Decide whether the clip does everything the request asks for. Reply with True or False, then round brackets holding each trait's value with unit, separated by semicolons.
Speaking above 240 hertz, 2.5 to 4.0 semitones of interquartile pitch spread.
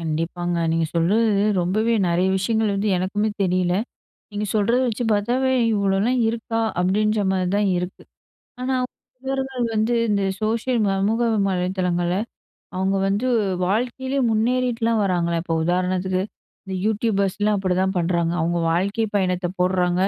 False (195 Hz; 3.6 semitones)